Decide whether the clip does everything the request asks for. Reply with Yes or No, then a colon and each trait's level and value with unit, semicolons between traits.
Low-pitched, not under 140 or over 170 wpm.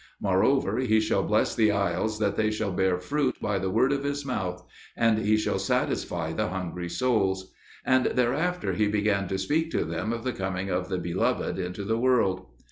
No: low, 105 Hz; average, 195 wpm